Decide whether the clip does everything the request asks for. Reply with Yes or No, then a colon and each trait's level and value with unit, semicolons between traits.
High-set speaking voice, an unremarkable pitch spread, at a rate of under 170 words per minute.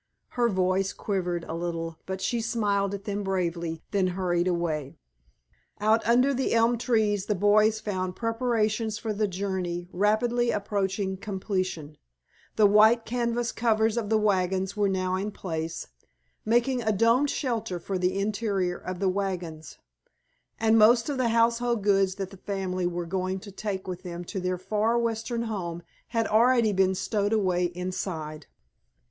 Yes: high, 200 Hz; average, 3.5 semitones; average, 160 wpm